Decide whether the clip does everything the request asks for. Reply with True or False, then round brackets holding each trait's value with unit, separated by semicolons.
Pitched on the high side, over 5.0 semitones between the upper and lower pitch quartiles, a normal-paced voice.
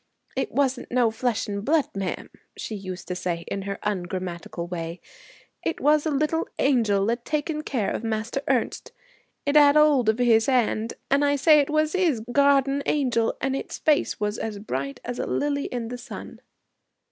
True (245 Hz; 5.6 semitones; 180 wpm)